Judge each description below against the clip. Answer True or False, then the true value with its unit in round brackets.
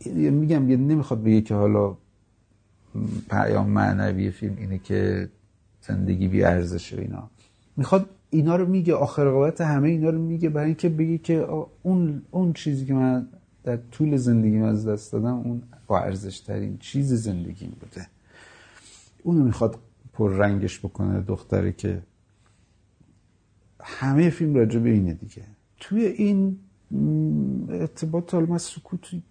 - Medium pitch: False (115 Hz)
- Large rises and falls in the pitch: True (7.0 semitones)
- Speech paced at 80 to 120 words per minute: False (135 wpm)